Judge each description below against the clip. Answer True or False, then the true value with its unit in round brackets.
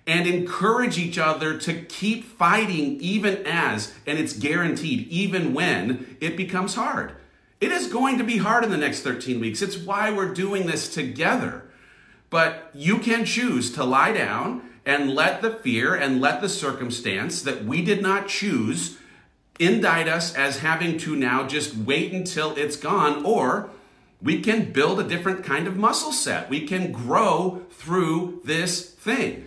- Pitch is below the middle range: False (175 Hz)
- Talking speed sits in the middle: True (165 wpm)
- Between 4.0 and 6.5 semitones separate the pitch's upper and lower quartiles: True (4.6 semitones)